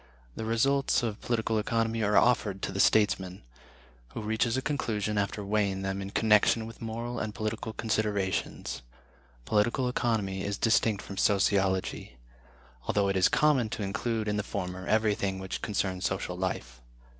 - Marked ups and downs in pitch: No, average, 2.7 semitones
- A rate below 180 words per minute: Yes, average, 155 wpm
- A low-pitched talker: Yes, low, 105 Hz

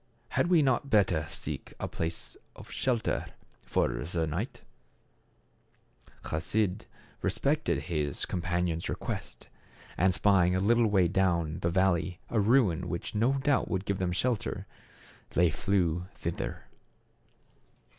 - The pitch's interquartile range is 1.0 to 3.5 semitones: No, average, 4.4 semitones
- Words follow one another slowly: Yes, slow, 125 wpm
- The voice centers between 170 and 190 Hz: No, very low, 95 Hz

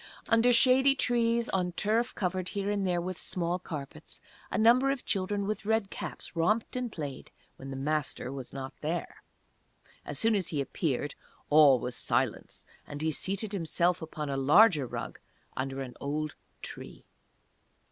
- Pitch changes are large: Yes, wide, 6.8 semitones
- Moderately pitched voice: Yes, medium, 180 Hz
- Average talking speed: Yes, average, 160 wpm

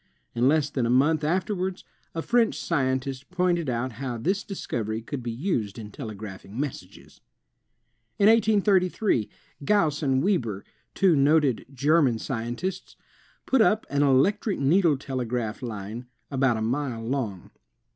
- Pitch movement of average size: No, wide, 7.1 semitones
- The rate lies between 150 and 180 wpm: No, average, 140 wpm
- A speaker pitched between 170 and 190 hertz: No, low, 135 Hz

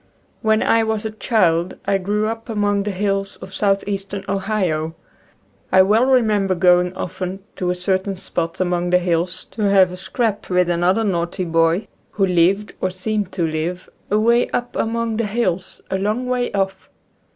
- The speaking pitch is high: Yes, high, 195 Hz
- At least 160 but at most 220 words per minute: Yes, average, 170 wpm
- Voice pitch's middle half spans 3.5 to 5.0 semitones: No, average, 3.0 semitones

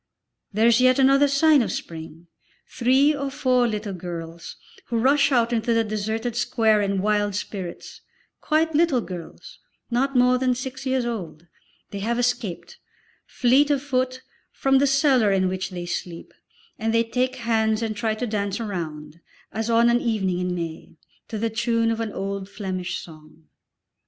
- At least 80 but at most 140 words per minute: No, average, 170 wpm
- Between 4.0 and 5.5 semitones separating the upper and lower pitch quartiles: Yes, average, 4.6 semitones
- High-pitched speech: Yes, high, 225 Hz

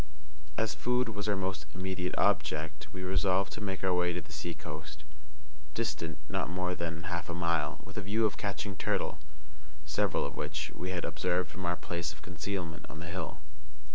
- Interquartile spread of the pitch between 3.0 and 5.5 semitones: No, narrow, 2.5 semitones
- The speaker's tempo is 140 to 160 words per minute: No, average, 185 wpm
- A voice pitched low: Yes, very low, 90 Hz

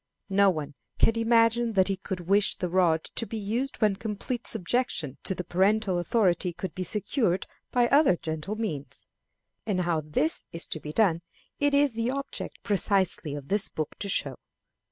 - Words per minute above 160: Yes, average, 175 wpm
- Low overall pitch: No, high, 195 Hz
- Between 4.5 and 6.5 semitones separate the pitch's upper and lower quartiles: Yes, average, 4.8 semitones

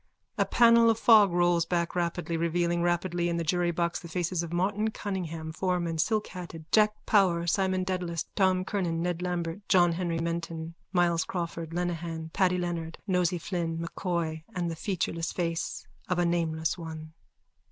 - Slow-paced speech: No, average, 155 wpm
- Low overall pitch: No, medium, 175 Hz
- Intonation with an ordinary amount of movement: No, narrow, 1.7 semitones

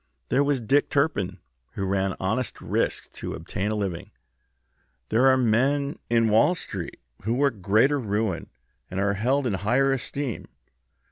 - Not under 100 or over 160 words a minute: Yes, average, 150 wpm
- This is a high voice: No, low, 115 Hz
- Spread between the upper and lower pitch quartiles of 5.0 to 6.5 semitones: Yes, average, 5.3 semitones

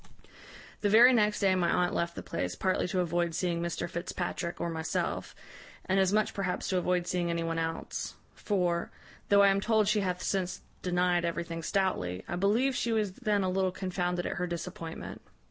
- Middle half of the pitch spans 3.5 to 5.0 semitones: No, narrow, 2.5 semitones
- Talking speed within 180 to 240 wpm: Yes, average, 190 wpm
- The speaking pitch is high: No, medium, 180 Hz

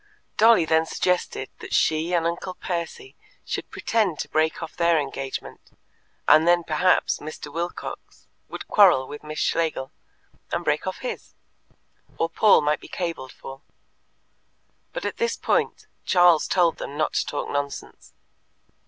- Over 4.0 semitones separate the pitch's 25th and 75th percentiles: No, average, 2.8 semitones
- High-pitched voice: No, medium, 165 Hz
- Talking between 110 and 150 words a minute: Yes, average, 145 wpm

